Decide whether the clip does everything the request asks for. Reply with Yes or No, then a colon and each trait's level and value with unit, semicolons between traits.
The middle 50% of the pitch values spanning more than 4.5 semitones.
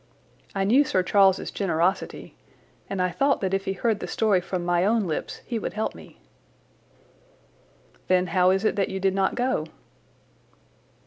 No: narrow, 2.6 semitones